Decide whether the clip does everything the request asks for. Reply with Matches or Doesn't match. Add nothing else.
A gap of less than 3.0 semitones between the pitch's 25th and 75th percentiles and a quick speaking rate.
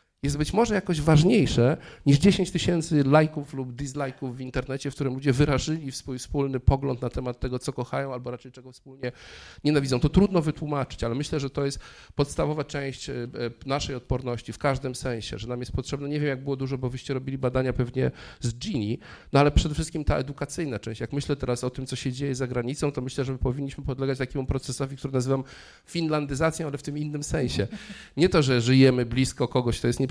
Matches